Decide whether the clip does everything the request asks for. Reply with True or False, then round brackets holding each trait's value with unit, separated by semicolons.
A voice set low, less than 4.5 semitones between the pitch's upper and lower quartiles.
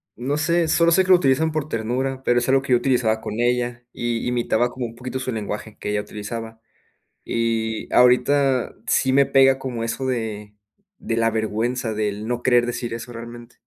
True (120 Hz; 2.7 semitones)